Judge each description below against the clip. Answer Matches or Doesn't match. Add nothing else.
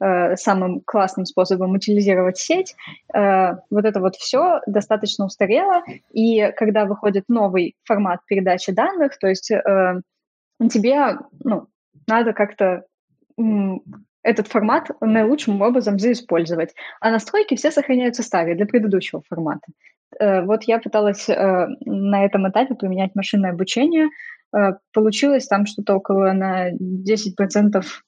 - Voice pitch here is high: Matches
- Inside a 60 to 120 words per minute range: Matches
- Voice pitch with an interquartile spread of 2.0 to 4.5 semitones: Matches